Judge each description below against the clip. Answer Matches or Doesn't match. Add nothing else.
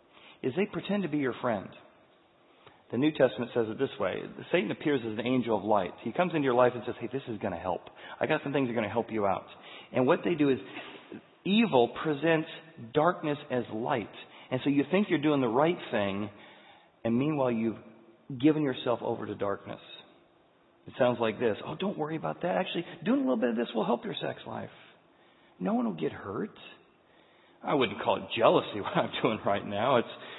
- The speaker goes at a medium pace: Doesn't match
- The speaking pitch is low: Matches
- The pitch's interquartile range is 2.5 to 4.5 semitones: Doesn't match